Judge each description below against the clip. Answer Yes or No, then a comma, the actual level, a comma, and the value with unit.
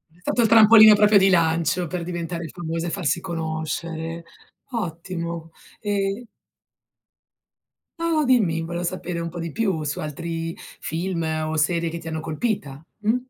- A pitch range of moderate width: Yes, average, 3.2 semitones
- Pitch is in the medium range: Yes, medium, 170 Hz